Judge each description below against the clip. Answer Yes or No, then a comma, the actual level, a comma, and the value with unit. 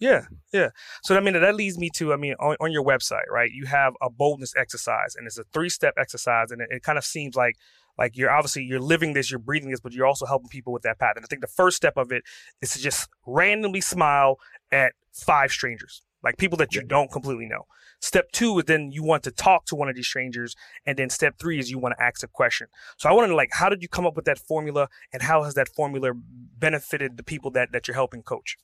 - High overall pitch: No, medium, 140 Hz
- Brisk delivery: Yes, fast, 260 wpm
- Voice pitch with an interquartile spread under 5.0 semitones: Yes, average, 3.7 semitones